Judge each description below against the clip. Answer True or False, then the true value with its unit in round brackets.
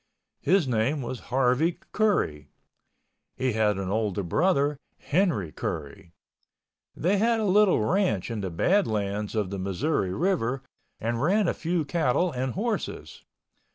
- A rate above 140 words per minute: False (135 wpm)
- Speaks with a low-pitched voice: True (130 Hz)